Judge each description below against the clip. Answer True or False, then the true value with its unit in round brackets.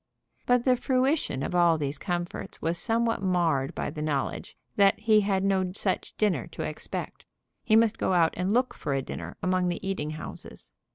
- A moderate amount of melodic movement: True (4.9 semitones)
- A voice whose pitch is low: False (185 Hz)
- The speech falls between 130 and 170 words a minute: False (185 wpm)